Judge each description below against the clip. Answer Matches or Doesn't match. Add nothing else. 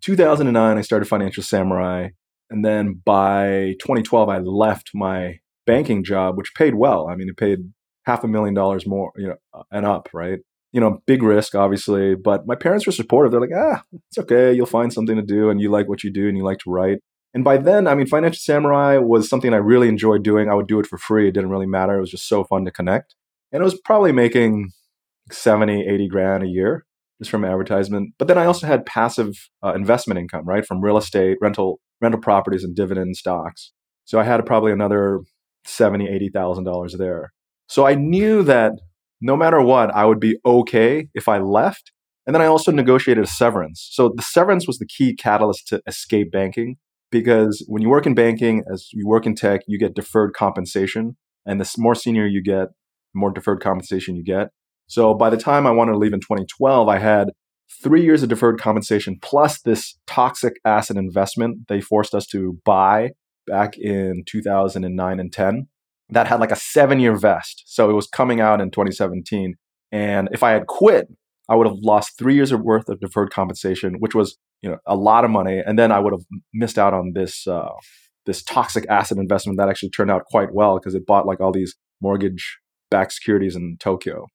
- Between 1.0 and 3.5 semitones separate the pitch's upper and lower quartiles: Matches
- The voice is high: Doesn't match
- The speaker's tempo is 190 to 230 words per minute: Matches